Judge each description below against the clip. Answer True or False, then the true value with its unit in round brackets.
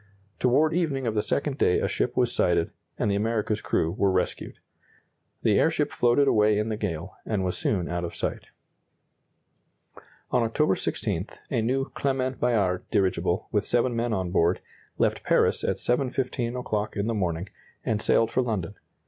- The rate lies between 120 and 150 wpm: False (170 wpm)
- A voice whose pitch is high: False (110 Hz)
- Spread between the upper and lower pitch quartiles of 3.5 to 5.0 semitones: True (4.7 semitones)